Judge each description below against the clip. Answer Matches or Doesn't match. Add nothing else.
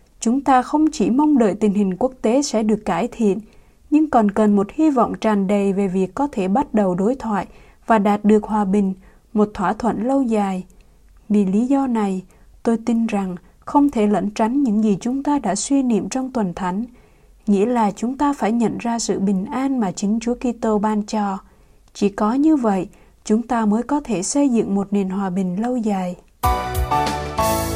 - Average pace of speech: Matches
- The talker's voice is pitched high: Matches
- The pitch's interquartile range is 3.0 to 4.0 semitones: Matches